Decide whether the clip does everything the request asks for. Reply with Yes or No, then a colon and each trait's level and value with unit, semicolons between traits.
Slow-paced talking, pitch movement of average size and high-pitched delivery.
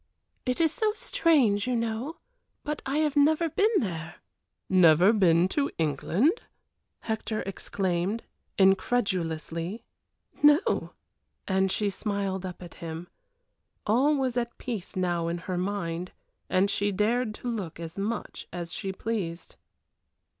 No: slow, 130 wpm; wide, 5.7 semitones; high, 200 Hz